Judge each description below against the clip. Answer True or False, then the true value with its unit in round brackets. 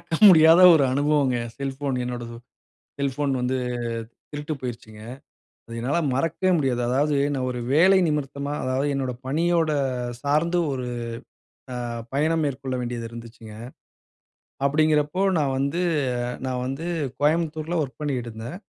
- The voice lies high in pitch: False (140 Hz)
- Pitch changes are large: False (3.4 semitones)